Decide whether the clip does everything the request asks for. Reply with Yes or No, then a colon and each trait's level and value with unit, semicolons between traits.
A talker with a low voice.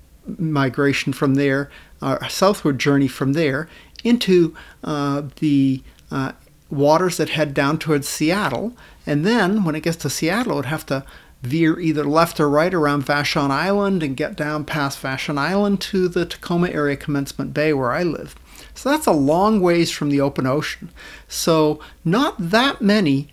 No: medium, 155 Hz